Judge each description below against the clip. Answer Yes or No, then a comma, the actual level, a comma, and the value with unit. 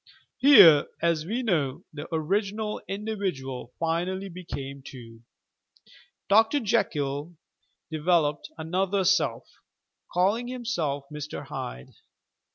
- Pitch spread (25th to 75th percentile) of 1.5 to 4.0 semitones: No, wide, 5.5 semitones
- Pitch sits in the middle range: Yes, medium, 170 Hz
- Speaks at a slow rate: Yes, slow, 90 wpm